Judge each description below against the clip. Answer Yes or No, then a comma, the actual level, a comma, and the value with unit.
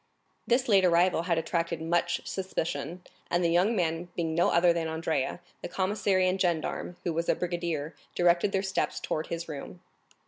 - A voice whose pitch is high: No, medium, 175 Hz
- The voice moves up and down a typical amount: No, narrow, 1.9 semitones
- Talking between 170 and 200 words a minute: Yes, average, 175 wpm